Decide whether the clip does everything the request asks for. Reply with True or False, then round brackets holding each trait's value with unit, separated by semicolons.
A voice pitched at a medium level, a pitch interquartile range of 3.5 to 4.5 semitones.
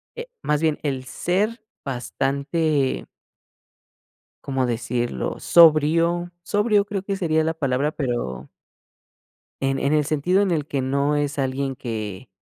True (145 Hz; 4.2 semitones)